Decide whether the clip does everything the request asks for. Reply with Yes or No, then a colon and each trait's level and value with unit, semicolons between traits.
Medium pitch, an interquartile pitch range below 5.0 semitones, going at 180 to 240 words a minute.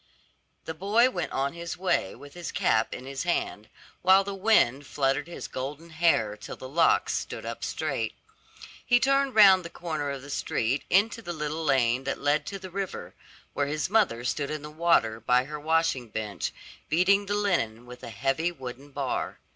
No: medium, 150 Hz; wide, 5.6 semitones; average, 185 wpm